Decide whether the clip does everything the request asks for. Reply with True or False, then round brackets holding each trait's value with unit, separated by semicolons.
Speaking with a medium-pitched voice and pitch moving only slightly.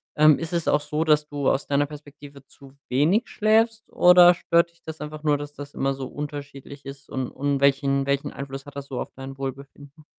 True (145 Hz; 1.9 semitones)